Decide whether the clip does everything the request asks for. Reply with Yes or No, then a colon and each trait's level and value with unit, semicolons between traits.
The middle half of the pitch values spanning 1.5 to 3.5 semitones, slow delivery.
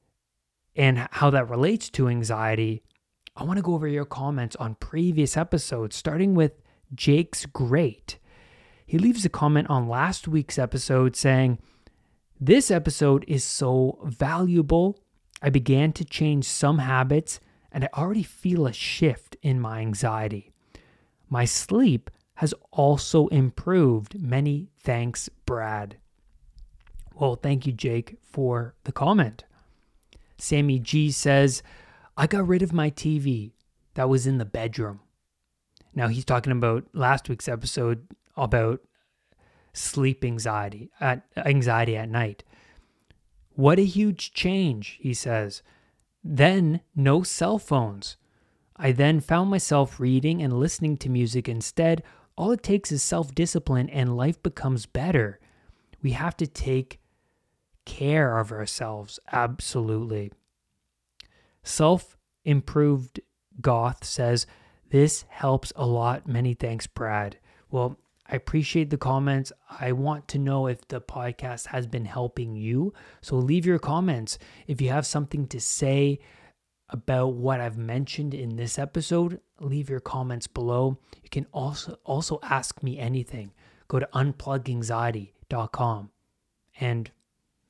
No: average, 4.2 semitones; slow, 125 wpm